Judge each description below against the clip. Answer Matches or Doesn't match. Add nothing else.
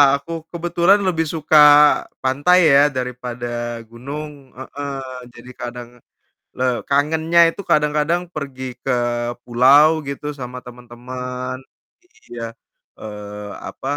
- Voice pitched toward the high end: Doesn't match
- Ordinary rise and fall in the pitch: Matches